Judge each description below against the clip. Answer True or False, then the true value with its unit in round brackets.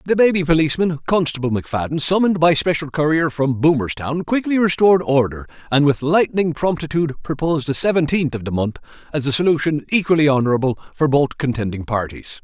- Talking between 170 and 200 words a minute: False (160 wpm)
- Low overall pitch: False (150 Hz)